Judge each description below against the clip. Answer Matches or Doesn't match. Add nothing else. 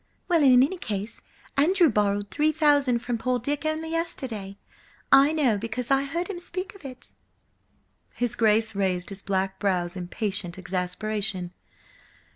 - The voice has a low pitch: Doesn't match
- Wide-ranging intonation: Matches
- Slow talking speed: Doesn't match